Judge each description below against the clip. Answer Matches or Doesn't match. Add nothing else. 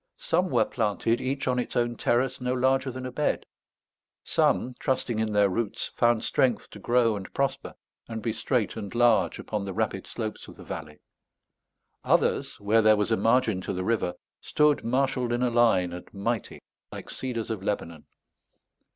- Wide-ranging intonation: Doesn't match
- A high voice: Doesn't match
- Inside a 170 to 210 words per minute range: Matches